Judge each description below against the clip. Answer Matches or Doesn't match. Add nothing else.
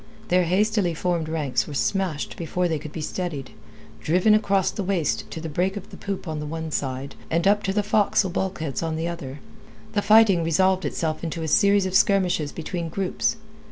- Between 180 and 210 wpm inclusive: Matches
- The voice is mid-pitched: Matches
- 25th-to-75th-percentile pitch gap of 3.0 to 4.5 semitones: Matches